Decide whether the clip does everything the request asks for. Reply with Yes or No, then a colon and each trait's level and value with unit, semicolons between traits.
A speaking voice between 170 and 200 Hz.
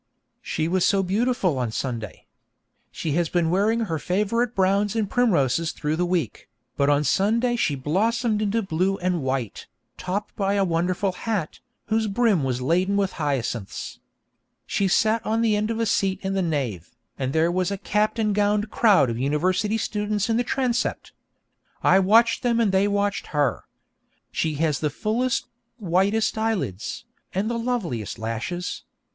Yes: high, 190 Hz